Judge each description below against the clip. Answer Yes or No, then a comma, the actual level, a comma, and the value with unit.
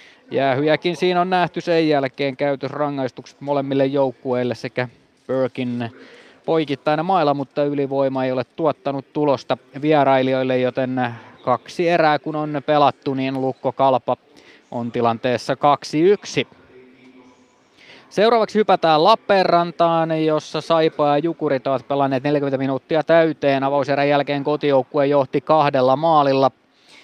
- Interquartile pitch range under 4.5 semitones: Yes, average, 2.7 semitones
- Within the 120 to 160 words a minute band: No, average, 110 wpm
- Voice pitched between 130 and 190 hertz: Yes, medium, 140 Hz